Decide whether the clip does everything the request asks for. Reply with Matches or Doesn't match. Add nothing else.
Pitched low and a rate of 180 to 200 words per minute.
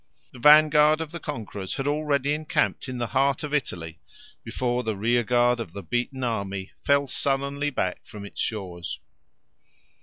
Doesn't match